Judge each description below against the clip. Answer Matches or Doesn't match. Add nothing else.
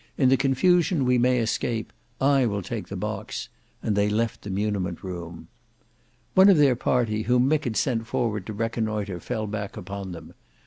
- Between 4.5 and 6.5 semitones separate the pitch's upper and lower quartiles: Doesn't match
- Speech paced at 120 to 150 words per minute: Doesn't match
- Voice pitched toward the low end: Matches